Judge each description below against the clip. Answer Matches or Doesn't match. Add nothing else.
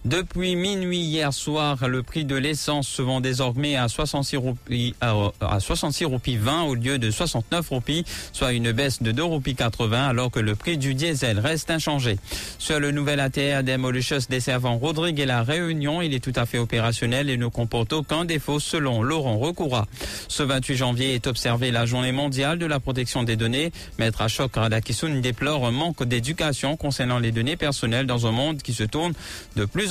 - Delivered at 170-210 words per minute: Matches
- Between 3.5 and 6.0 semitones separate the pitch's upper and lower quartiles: Matches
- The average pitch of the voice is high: Doesn't match